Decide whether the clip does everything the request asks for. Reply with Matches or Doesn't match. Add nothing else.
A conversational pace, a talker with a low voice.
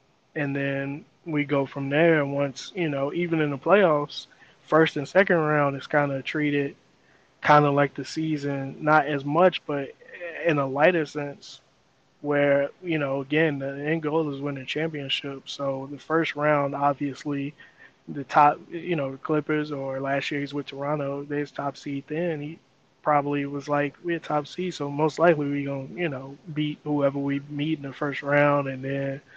Doesn't match